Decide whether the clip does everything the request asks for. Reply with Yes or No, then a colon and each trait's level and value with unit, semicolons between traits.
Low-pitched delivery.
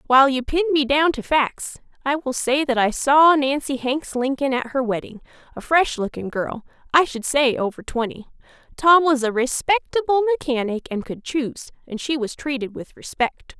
No: very high, 270 Hz